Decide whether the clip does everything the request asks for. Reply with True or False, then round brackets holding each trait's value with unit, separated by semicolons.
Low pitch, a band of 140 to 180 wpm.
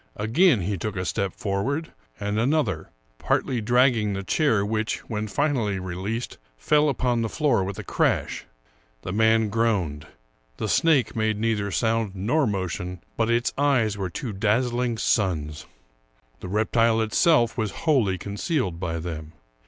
True (110 Hz; 150 wpm)